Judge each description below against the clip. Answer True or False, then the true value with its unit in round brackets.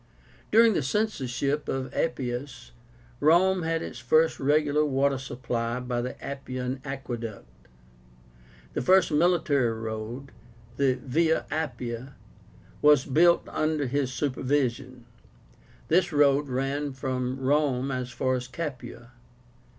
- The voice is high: False (135 Hz)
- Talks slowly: True (120 wpm)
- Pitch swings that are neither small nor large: True (3.1 semitones)